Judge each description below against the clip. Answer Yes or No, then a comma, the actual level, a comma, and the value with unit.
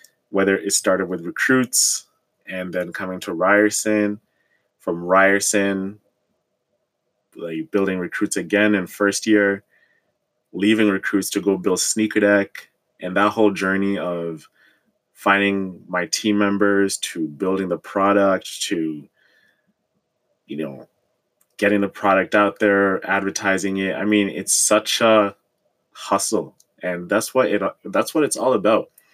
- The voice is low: Yes, low, 100 Hz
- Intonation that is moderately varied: No, narrow, 1.3 semitones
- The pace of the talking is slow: Yes, slow, 130 wpm